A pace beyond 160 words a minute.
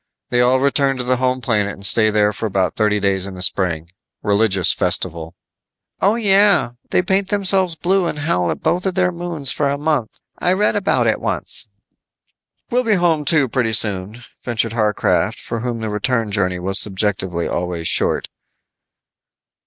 Yes: average, 175 wpm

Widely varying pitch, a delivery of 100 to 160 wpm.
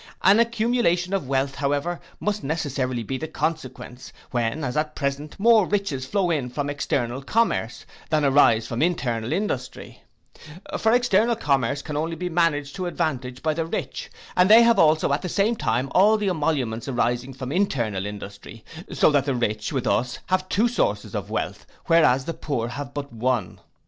No: wide, 6.0 semitones; average, 175 wpm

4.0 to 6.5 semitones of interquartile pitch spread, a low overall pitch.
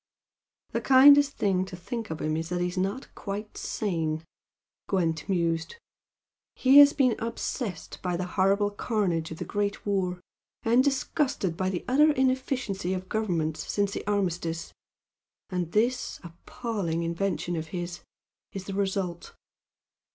No: average, 4.6 semitones; high, 195 Hz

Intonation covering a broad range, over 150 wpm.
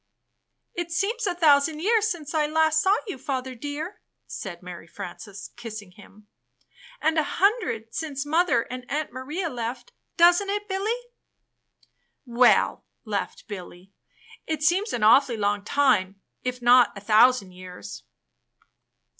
No: wide, 7.8 semitones; slow, 135 wpm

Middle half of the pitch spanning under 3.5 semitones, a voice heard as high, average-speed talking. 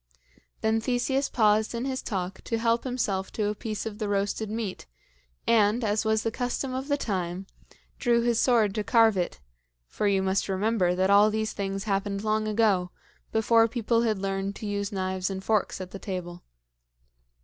Yes: average, 2.8 semitones; high, 215 Hz; average, 180 wpm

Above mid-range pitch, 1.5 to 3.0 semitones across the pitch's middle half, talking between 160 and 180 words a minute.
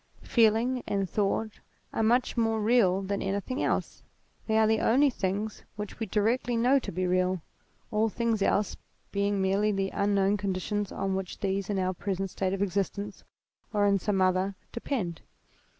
Yes: high, 200 Hz; narrow, 2.4 semitones; average, 170 wpm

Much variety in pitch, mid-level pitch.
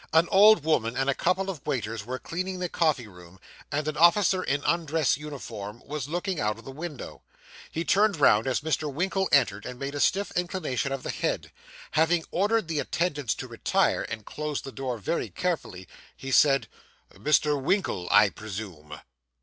Yes: wide, 6.2 semitones; medium, 145 Hz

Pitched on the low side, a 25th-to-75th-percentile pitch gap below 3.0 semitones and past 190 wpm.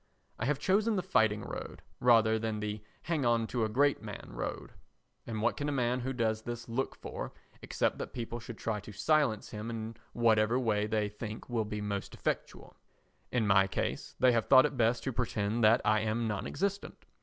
Yes: low, 115 Hz; narrow, 2.6 semitones; average, 200 wpm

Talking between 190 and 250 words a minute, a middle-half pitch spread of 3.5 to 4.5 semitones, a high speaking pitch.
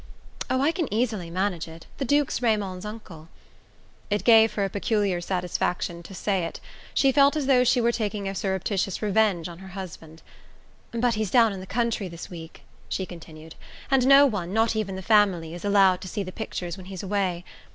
Yes: average, 195 wpm; average, 4.0 semitones; high, 200 Hz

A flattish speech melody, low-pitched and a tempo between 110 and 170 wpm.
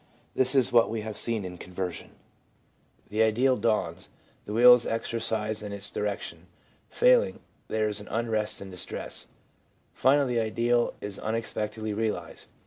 Yes: narrow, 2.1 semitones; low, 110 Hz; average, 140 wpm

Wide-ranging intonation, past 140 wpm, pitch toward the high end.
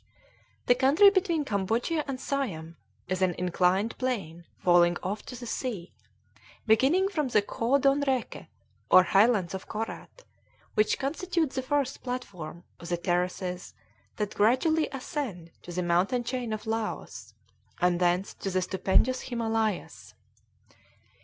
No: wide, 6.4 semitones; slow, 135 wpm; high, 220 Hz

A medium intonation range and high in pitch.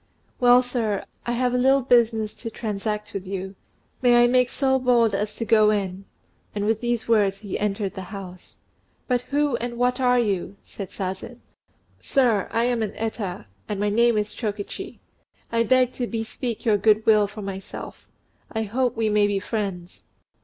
Yes: average, 3.1 semitones; high, 220 Hz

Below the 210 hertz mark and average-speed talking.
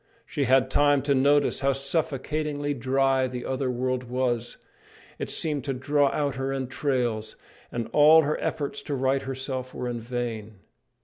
Yes: low, 135 Hz; average, 160 wpm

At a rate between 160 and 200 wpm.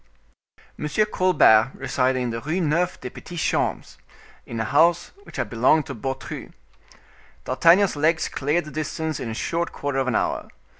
Yes: average, 165 wpm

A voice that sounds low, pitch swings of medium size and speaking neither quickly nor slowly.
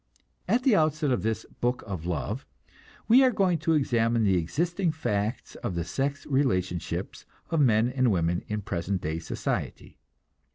No: low, 120 Hz; wide, 8.5 semitones; average, 160 wpm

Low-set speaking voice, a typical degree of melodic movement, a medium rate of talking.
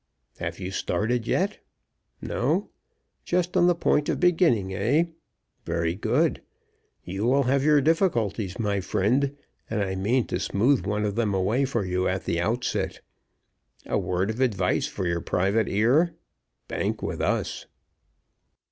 No: low, 110 Hz; wide, 6.4 semitones; average, 145 wpm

